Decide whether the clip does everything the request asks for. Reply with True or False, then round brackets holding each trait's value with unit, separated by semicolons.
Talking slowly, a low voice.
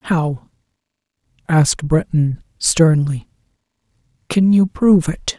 False (90 wpm; 160 Hz)